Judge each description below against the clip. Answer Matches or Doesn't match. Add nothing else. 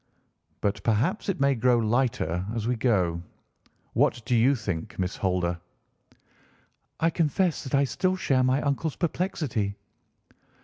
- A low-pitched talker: Matches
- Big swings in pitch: Matches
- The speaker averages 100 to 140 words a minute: Matches